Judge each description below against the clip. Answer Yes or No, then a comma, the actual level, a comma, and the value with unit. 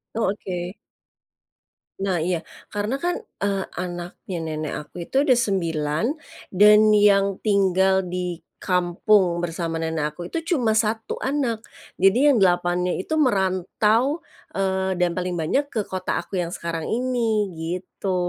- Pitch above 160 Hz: Yes, high, 190 Hz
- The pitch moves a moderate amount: Yes, average, 3.4 semitones